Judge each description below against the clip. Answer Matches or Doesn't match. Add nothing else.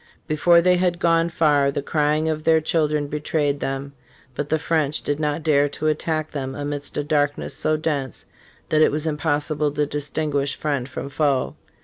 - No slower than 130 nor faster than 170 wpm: Doesn't match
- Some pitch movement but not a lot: Doesn't match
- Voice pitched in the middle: Matches